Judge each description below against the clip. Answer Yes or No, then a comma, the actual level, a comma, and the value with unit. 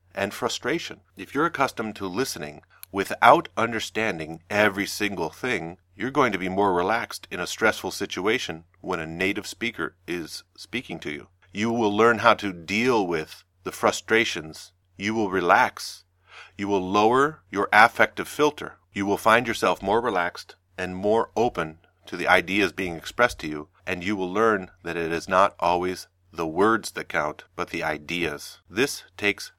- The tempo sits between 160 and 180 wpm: Yes, average, 170 wpm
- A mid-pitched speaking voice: No, very low, 95 Hz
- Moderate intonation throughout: Yes, average, 3.5 semitones